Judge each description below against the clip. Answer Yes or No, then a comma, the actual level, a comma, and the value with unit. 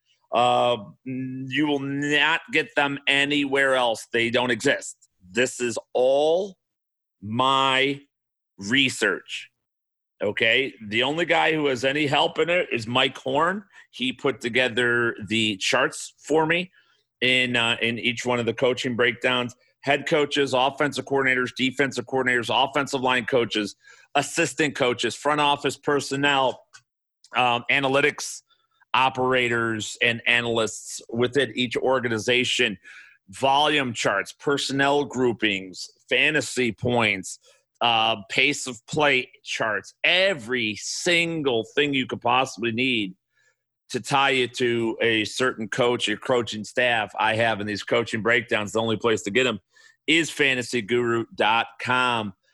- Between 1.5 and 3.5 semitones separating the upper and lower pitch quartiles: Yes, average, 3.2 semitones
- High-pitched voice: No, low, 125 Hz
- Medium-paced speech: No, slow, 125 wpm